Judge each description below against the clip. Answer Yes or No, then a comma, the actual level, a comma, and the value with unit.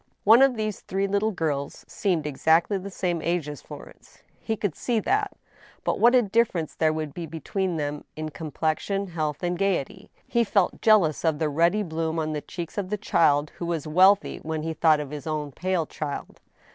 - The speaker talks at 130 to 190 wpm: No, average, 200 wpm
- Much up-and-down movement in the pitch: No, average, 4.3 semitones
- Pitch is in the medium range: Yes, medium, 170 Hz